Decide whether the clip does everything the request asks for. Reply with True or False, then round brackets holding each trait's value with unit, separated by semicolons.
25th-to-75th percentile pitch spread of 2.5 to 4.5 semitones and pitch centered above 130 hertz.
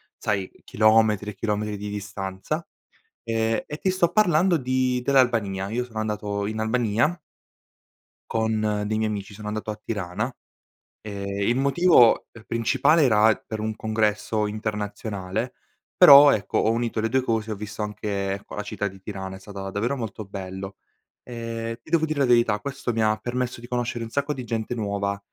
False (2.9 semitones; 110 Hz)